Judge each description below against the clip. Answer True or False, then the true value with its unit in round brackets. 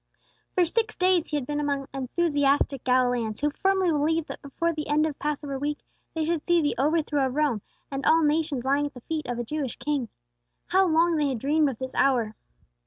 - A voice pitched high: True (295 Hz)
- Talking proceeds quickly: True (210 wpm)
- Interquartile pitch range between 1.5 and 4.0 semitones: True (2.9 semitones)